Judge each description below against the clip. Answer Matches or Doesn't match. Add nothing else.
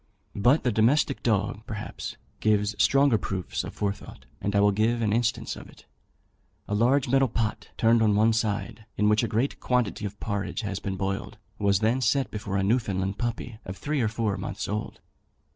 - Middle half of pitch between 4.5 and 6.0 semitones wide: Doesn't match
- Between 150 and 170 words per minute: Doesn't match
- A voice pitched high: Doesn't match